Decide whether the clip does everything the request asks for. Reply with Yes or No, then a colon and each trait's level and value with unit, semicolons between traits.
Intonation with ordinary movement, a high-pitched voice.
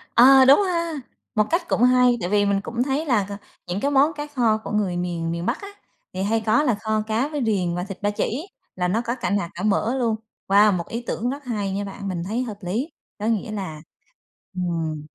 Yes: average, 4.8 semitones; high, 215 Hz